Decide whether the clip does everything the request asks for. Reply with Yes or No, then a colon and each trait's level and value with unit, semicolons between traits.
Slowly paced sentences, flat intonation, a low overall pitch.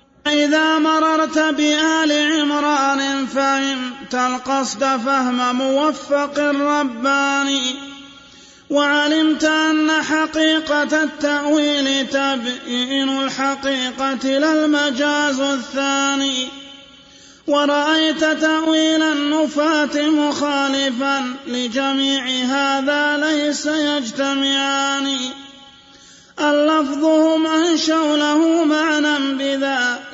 No: slow, 60 wpm; narrow, 1.8 semitones; very high, 285 Hz